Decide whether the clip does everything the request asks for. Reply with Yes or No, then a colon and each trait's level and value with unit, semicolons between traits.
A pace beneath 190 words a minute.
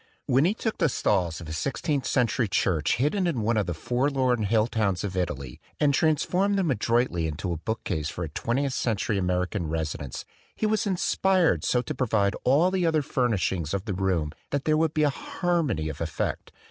No: average, 200 wpm